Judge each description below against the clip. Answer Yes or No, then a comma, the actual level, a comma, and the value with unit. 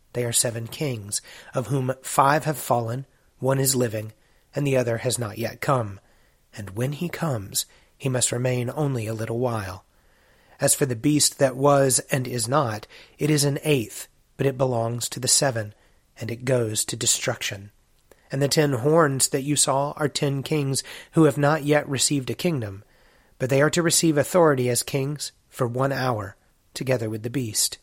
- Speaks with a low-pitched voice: Yes, low, 130 Hz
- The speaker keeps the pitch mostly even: No, average, 3.8 semitones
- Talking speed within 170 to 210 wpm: Yes, average, 185 wpm